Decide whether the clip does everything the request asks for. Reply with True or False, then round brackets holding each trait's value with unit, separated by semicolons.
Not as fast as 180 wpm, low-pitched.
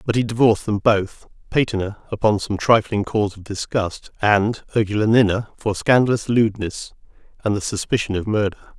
True (150 wpm; 105 Hz)